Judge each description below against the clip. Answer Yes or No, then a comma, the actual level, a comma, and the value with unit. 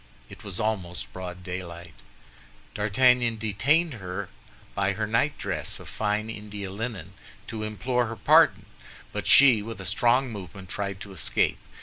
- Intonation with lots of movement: No, average, 3.3 semitones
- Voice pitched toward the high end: No, low, 105 Hz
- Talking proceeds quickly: No, average, 145 wpm